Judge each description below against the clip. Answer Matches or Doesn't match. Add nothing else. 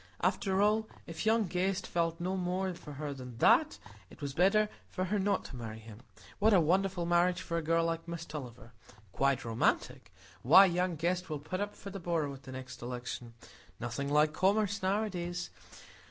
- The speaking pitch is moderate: Matches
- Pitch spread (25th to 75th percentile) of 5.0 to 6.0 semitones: Matches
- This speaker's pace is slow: Doesn't match